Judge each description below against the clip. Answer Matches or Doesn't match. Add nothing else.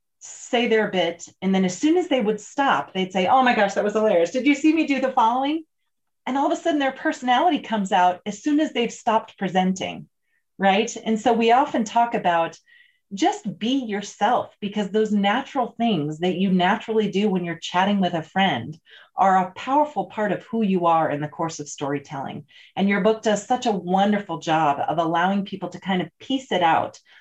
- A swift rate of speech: Matches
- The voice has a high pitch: Matches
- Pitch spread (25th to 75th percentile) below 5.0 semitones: Doesn't match